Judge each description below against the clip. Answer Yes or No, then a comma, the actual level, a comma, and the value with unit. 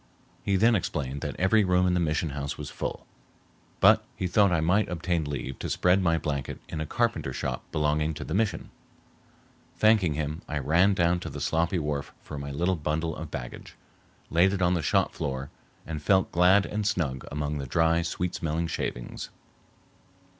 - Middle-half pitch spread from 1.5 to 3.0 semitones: No, average, 3.5 semitones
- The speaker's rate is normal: Yes, average, 185 wpm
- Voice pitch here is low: Yes, very low, 80 Hz